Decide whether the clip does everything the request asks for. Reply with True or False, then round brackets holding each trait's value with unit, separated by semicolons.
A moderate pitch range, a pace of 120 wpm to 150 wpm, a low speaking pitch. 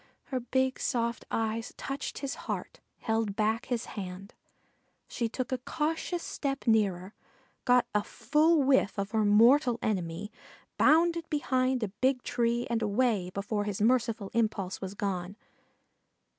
False (4.0 semitones; 140 wpm; 230 Hz)